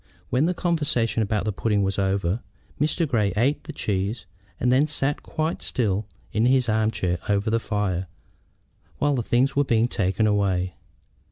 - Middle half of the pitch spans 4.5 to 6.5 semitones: Yes, average, 4.9 semitones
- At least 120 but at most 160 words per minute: No, average, 170 wpm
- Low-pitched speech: Yes, low, 110 Hz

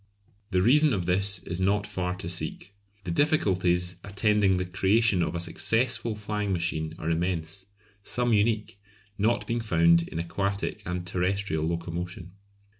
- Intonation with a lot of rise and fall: No, average, 3.2 semitones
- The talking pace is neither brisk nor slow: Yes, average, 145 wpm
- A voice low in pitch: Yes, very low, 95 Hz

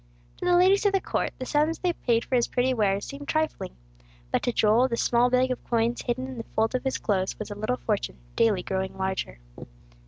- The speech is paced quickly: Yes, fast, 225 wpm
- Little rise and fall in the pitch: No, average, 3.7 semitones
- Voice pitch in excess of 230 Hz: Yes, high, 240 Hz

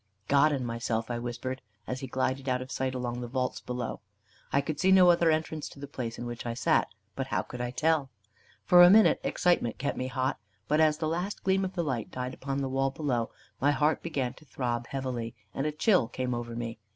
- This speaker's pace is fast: Yes, fast, 230 wpm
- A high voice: No, low, 130 Hz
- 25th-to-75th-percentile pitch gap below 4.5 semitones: Yes, average, 3.9 semitones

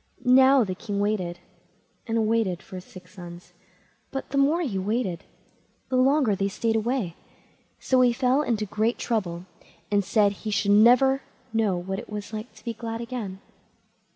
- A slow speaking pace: No, average, 165 wpm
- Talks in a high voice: Yes, high, 220 Hz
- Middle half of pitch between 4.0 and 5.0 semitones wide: Yes, average, 4.3 semitones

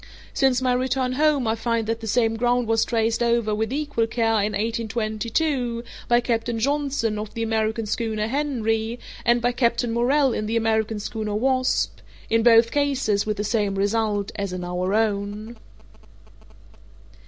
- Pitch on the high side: Yes, high, 225 Hz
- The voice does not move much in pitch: Yes, narrow, 2.1 semitones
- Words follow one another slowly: No, average, 155 wpm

